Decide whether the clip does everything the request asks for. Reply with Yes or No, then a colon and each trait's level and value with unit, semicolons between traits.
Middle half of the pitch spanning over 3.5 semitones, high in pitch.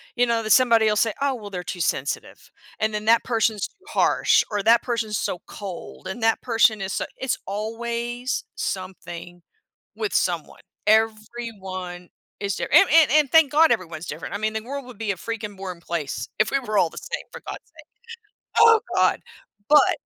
Yes: average, 3.9 semitones; high, 220 Hz